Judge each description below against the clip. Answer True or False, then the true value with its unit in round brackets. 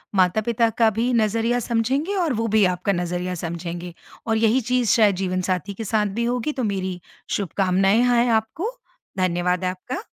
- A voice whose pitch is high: True (215 Hz)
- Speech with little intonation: False (4.4 semitones)